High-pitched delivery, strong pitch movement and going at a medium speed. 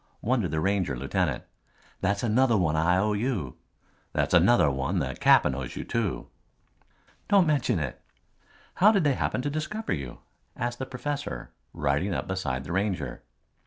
No: low, 100 Hz; wide, 9.0 semitones; average, 160 wpm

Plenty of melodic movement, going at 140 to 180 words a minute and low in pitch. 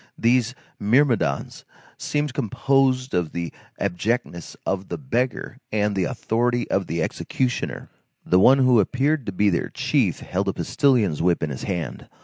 Yes: wide, 5.9 semitones; average, 150 wpm; low, 110 Hz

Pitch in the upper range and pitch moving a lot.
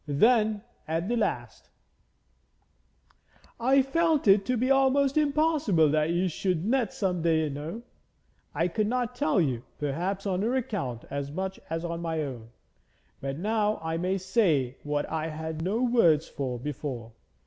No: medium, 180 Hz; wide, 7.0 semitones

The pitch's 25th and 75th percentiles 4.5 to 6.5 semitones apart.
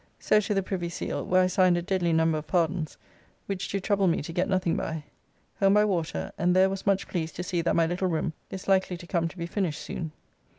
No: narrow, 2.5 semitones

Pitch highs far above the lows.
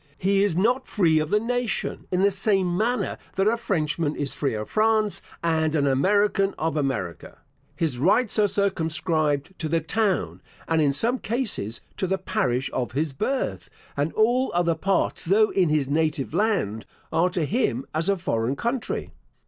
Yes: wide, 5.7 semitones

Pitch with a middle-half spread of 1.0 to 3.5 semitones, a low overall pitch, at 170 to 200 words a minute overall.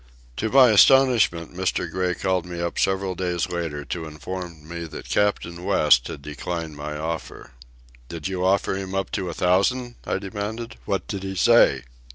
Yes: average, 2.8 semitones; very low, 90 Hz; average, 175 wpm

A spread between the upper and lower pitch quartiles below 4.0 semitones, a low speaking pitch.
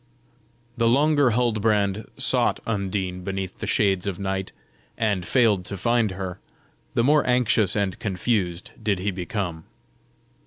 Yes: average, 3.4 semitones; low, 100 Hz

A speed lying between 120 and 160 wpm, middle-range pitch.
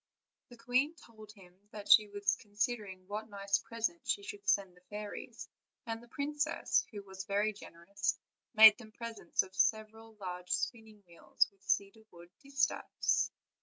No: average, 150 wpm; high, 215 Hz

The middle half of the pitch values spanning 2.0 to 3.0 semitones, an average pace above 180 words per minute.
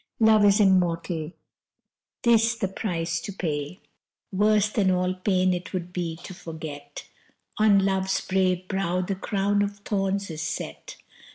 No: narrow, 2.6 semitones; average, 145 wpm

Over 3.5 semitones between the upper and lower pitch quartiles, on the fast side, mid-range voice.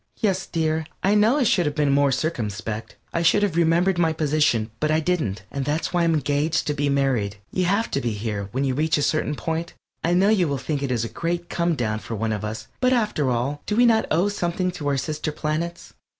Yes: average, 4.7 semitones; fast, 235 wpm; medium, 155 Hz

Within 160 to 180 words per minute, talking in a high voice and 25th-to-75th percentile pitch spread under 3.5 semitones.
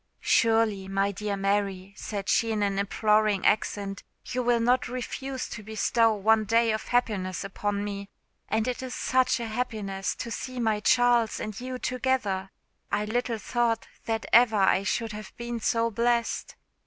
Yes: average, 165 wpm; high, 220 Hz; average, 2.9 semitones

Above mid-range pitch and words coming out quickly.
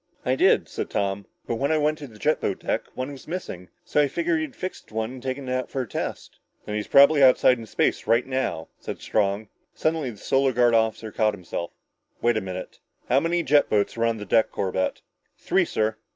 No: low, 120 Hz; fast, 225 wpm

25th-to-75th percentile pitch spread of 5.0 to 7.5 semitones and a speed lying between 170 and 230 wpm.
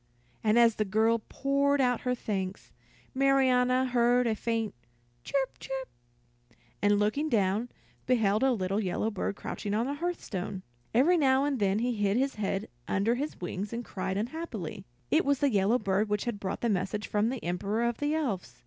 No: average, 4.4 semitones; average, 180 wpm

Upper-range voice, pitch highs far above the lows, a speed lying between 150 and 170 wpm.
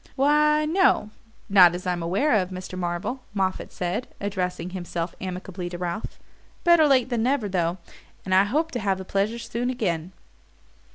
Yes: high, 195 Hz; wide, 5.8 semitones; average, 165 wpm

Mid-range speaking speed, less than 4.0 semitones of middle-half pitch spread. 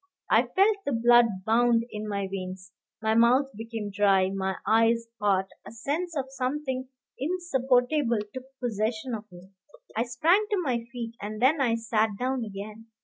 Yes: average, 160 wpm; average, 3.6 semitones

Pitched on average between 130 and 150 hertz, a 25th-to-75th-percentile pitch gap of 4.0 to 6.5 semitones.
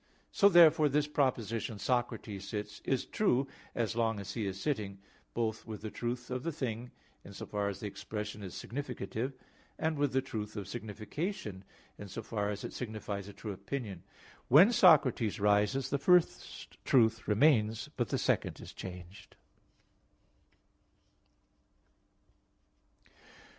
No: low, 115 Hz; average, 4.5 semitones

